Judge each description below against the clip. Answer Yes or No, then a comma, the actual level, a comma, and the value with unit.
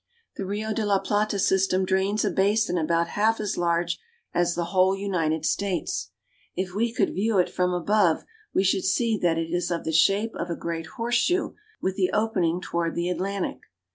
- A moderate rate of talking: Yes, average, 190 wpm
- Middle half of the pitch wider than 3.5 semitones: No, average, 3.1 semitones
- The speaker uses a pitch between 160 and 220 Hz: Yes, high, 190 Hz